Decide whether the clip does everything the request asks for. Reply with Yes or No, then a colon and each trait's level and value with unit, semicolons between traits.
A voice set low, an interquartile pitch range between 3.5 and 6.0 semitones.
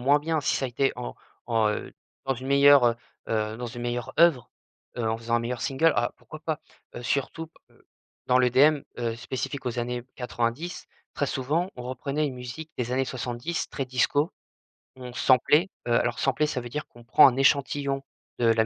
No: low, 130 Hz; average, 2.9 semitones